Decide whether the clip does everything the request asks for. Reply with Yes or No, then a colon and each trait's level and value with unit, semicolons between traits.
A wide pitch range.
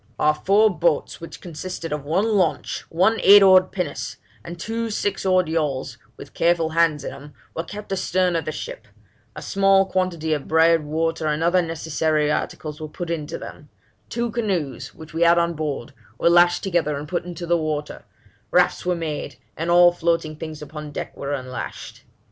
No: average, 3.2 semitones